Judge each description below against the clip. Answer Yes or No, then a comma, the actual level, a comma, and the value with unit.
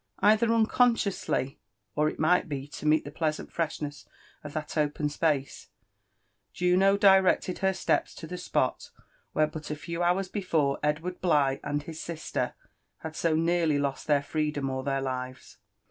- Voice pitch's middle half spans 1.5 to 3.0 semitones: No, average, 3.5 semitones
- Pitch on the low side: No, medium, 155 Hz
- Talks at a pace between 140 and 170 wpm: Yes, average, 160 wpm